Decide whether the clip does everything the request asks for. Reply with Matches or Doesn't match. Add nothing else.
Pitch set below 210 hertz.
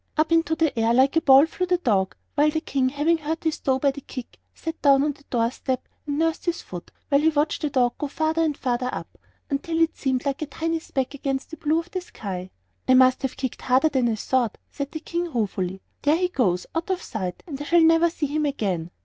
Doesn't match